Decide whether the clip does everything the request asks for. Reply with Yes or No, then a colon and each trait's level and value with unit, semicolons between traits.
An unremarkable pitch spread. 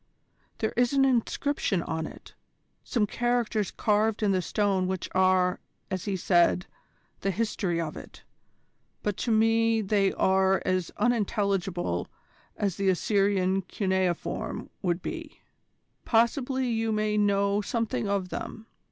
Yes: average, 3.1 semitones